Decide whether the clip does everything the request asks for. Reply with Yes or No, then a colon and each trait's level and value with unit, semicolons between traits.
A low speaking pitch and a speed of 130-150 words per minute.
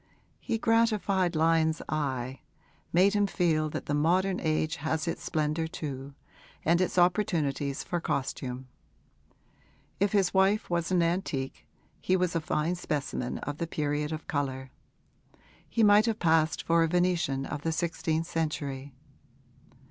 No: medium, 160 Hz; average, 140 wpm